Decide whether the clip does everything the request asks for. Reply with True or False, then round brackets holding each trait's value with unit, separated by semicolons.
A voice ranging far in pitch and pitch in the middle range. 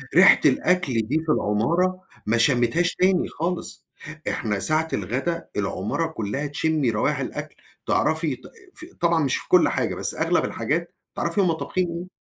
True (6.6 semitones; 160 Hz)